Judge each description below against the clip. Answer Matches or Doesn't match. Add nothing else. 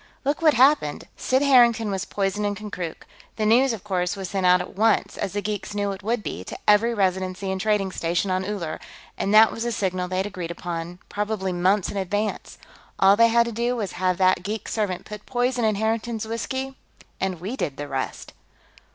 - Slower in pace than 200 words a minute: Doesn't match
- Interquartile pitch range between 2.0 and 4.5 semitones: Matches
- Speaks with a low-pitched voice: Doesn't match